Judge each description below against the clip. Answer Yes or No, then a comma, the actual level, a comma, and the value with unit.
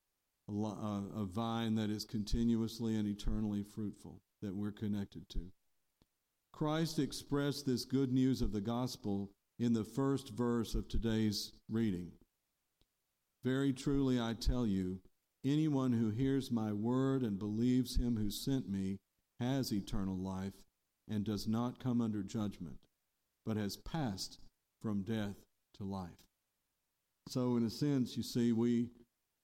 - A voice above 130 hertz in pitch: No, low, 110 Hz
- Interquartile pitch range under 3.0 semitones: No, average, 3.5 semitones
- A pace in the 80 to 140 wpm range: Yes, slow, 135 wpm